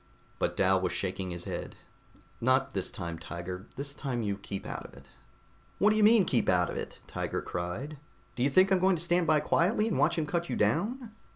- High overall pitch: No, low, 135 Hz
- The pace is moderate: No, fast, 220 wpm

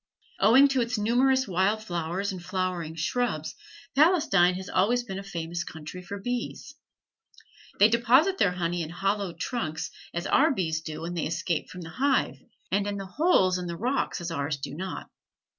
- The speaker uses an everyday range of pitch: No, wide, 5.7 semitones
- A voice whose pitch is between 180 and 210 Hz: Yes, high, 190 Hz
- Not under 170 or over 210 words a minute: Yes, average, 175 wpm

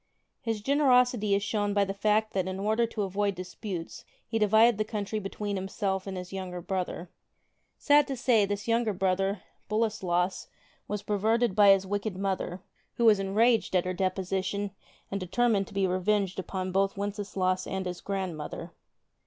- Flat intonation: Yes, narrow, 2.2 semitones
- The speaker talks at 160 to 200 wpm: Yes, average, 165 wpm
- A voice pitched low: No, high, 200 Hz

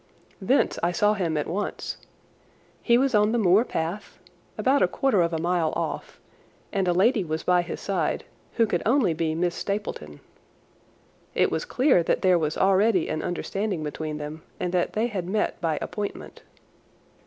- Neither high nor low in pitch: Yes, medium, 180 Hz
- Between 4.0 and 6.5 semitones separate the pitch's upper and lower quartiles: Yes, average, 4.4 semitones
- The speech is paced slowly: No, average, 175 wpm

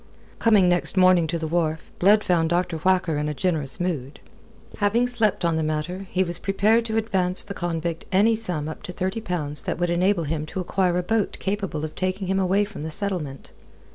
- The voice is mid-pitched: Yes, medium, 180 Hz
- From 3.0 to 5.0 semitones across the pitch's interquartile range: Yes, average, 3.4 semitones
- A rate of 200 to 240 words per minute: Yes, fast, 205 wpm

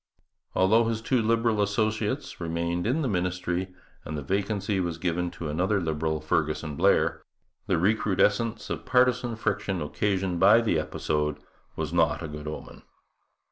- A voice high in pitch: No, very low, 95 Hz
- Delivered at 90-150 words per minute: Yes, average, 145 wpm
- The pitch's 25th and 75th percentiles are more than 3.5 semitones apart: Yes, average, 4.9 semitones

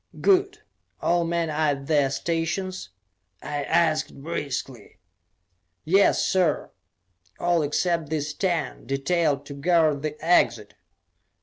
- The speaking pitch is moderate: Yes, medium, 160 Hz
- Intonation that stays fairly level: No, average, 3.3 semitones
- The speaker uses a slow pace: Yes, slow, 110 wpm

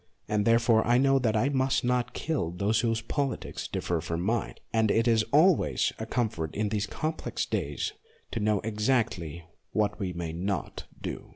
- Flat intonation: No, average, 3.7 semitones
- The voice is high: No, low, 110 Hz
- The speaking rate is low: No, average, 175 wpm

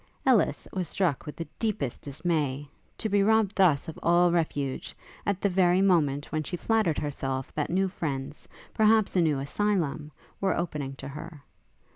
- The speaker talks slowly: No, average, 165 wpm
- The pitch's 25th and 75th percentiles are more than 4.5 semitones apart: Yes, average, 5.0 semitones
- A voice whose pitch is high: No, medium, 170 Hz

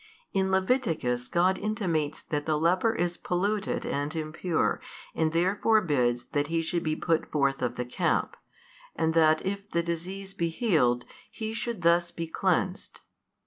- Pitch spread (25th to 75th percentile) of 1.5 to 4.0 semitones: Yes, average, 3.6 semitones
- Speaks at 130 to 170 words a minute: Yes, average, 155 wpm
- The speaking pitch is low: No, medium, 170 Hz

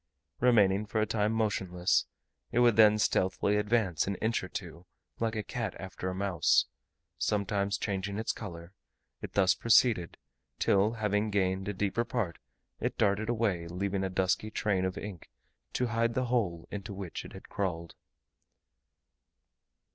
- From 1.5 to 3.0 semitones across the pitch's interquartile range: Yes, average, 2.7 semitones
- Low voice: Yes, low, 100 Hz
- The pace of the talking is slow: No, average, 155 wpm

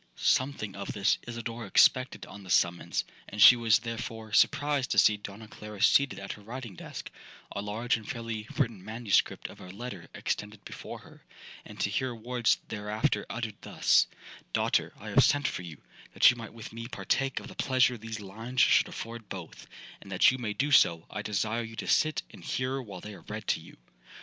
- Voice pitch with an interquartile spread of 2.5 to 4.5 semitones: Yes, average, 2.9 semitones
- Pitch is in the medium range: No, low, 110 Hz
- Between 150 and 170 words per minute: No, average, 195 wpm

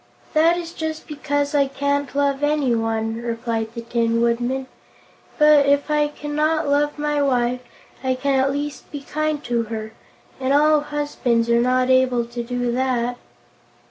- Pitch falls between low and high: No, very high, 270 Hz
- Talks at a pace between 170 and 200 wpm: No, average, 155 wpm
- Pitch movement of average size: Yes, average, 3.6 semitones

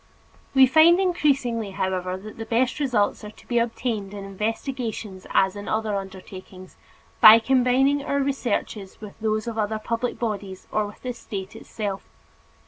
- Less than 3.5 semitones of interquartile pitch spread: No, average, 3.9 semitones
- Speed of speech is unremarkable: Yes, average, 155 wpm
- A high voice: Yes, high, 220 Hz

